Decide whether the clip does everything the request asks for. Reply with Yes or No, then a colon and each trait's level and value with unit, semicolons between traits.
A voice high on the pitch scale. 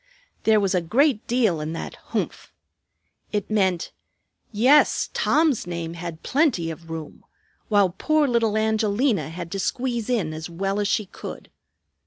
Yes: high, 205 Hz